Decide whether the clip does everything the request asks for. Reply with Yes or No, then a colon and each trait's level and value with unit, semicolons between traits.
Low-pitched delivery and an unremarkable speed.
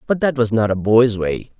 No: low, 115 Hz; fast, 265 wpm